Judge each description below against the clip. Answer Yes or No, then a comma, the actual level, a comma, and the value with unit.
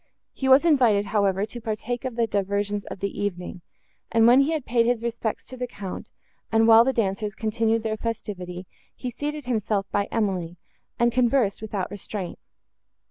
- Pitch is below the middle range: No, high, 220 Hz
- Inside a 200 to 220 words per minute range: No, average, 175 wpm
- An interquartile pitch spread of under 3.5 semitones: Yes, average, 3.0 semitones